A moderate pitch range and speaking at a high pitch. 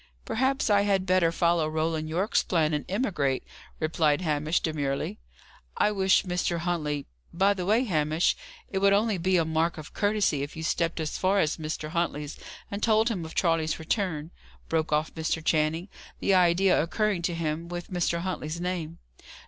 No: average, 3.3 semitones; medium, 170 Hz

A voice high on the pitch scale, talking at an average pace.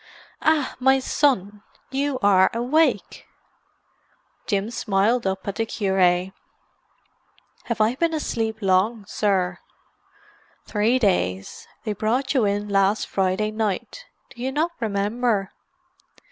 No: high, 215 Hz; slow, 115 wpm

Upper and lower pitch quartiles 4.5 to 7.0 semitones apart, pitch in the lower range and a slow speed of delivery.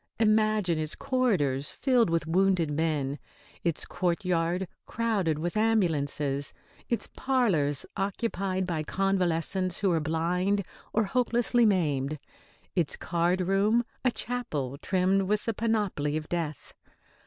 No: average, 5.1 semitones; medium, 185 Hz; slow, 120 wpm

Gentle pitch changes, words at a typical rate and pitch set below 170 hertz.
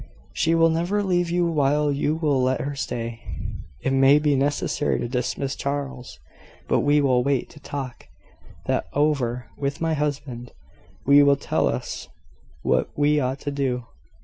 Yes: narrow, 2.3 semitones; average, 160 wpm; medium, 140 Hz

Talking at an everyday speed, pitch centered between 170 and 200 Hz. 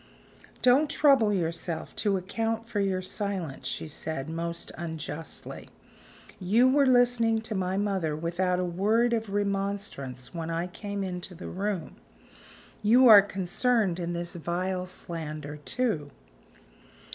No: slow, 130 wpm; high, 190 Hz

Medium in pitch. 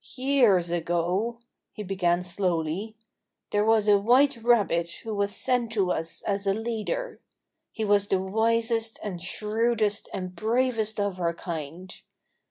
No: high, 205 Hz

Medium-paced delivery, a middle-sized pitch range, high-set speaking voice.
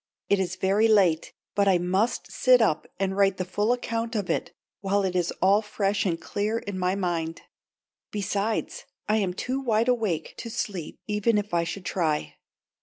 Yes: average, 180 wpm; average, 3.0 semitones; high, 200 Hz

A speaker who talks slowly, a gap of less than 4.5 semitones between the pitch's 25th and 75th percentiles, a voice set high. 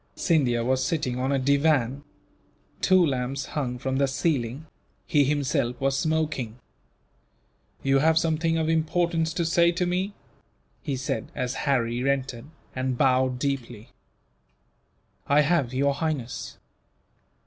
No: slow, 125 wpm; average, 3.8 semitones; medium, 140 Hz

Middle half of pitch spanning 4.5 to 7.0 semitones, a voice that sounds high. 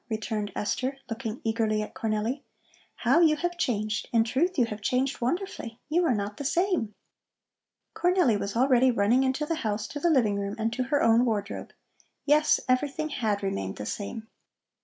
Yes: average, 5.2 semitones; high, 235 Hz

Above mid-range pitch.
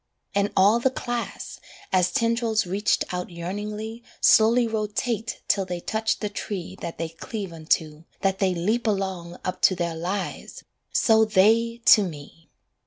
Yes: high, 200 Hz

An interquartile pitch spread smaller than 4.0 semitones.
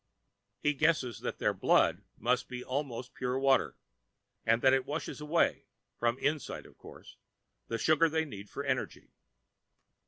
Yes: average, 3.3 semitones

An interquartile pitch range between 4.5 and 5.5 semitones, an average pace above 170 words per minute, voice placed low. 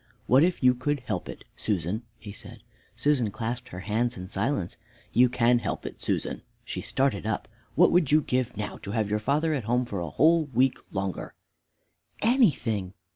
Yes: average, 4.9 semitones; average, 180 wpm; low, 120 Hz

